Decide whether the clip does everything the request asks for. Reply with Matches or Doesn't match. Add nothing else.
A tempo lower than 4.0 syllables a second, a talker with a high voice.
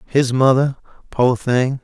Doesn't match